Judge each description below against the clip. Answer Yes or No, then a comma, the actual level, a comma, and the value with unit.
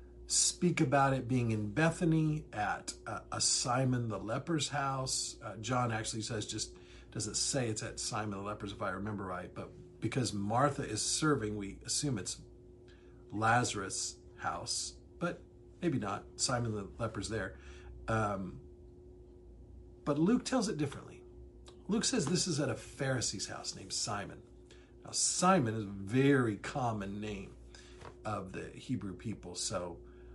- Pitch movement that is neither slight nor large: No, wide, 5.9 semitones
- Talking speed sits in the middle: Yes, average, 145 wpm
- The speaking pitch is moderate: No, low, 110 Hz